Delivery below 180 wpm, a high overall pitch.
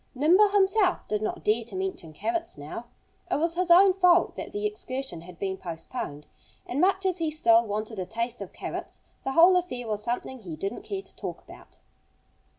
No: average, 195 wpm; very high, 260 Hz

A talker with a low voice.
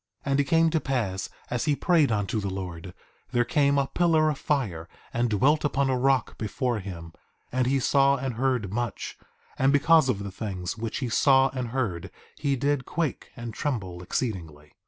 Yes: low, 125 Hz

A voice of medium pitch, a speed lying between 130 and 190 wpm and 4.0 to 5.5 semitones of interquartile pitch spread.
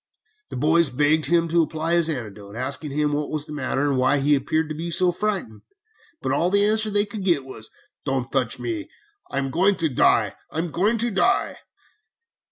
No: medium, 155 Hz; average, 200 wpm; average, 4.8 semitones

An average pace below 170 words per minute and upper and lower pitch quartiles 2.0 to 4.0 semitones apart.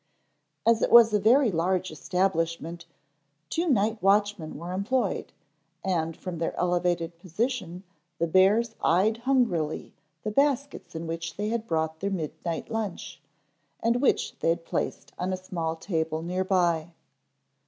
No: average, 145 wpm; average, 4.7 semitones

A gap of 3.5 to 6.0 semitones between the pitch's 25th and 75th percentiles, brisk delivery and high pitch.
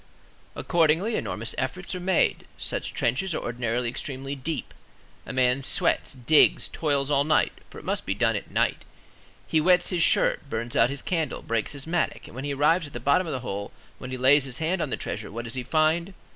No: average, 4.7 semitones; fast, 210 wpm; medium, 140 Hz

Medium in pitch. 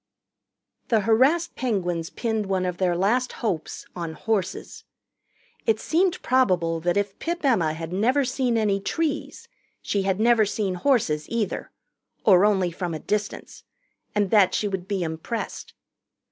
No: high, 205 Hz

